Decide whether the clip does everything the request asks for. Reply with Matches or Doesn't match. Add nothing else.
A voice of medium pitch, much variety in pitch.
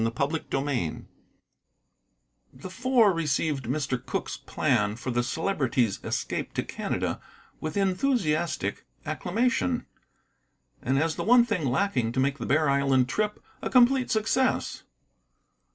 Matches